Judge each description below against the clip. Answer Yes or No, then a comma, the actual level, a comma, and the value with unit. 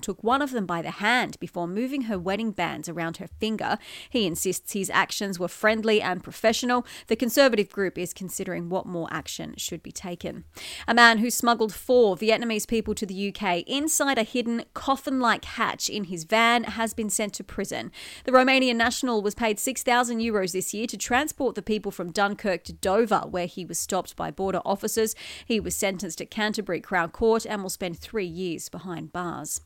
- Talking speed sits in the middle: Yes, average, 195 wpm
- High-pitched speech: Yes, high, 210 Hz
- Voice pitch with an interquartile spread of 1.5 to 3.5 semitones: No, average, 4.2 semitones